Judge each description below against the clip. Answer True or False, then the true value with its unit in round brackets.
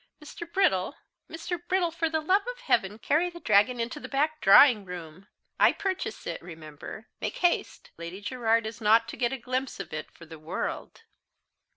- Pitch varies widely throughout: True (8.9 semitones)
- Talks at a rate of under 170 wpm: False (185 wpm)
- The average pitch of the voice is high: True (235 Hz)